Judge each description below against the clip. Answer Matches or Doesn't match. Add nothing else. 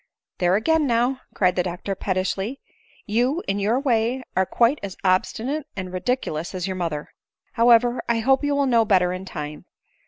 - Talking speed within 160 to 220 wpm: Matches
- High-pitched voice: Matches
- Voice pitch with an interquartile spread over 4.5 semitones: Matches